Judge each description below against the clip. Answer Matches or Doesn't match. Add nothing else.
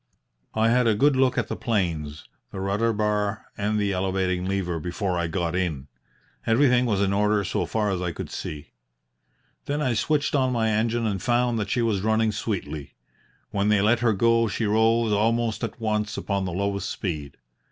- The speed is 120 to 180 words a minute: Doesn't match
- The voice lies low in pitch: Matches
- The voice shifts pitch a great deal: Doesn't match